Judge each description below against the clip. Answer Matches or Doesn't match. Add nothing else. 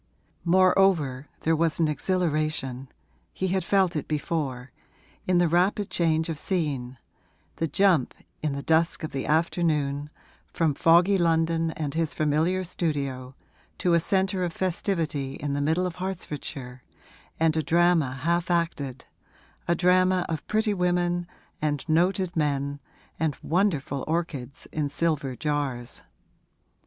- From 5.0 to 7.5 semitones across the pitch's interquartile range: Doesn't match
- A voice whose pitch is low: Doesn't match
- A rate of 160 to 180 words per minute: Doesn't match